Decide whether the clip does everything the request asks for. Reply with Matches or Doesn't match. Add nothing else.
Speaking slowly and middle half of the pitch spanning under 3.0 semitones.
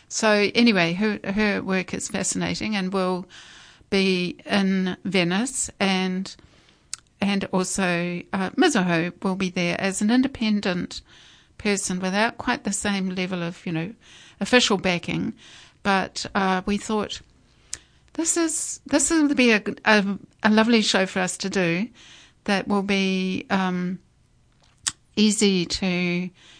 Matches